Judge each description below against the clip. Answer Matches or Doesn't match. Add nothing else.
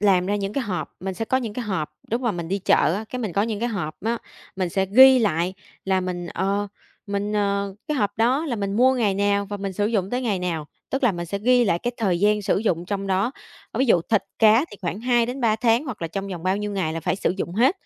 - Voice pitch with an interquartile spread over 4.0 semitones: Doesn't match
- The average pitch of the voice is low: Doesn't match